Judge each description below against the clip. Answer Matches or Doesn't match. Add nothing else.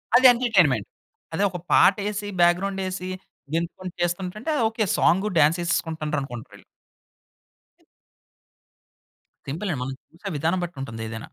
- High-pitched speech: Doesn't match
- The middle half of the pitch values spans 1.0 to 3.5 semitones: Doesn't match